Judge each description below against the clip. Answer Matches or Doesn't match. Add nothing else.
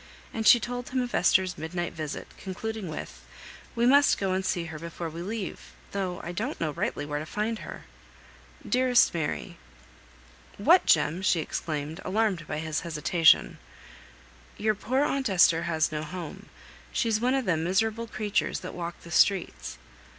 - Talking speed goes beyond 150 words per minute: Matches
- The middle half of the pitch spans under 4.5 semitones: Doesn't match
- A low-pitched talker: Doesn't match